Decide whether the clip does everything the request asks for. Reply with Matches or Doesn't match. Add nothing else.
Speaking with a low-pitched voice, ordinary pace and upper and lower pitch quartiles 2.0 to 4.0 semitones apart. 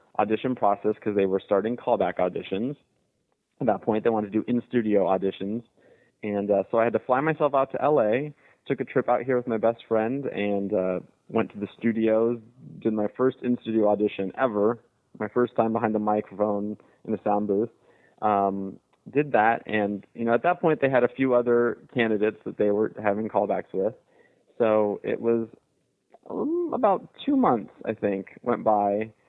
Matches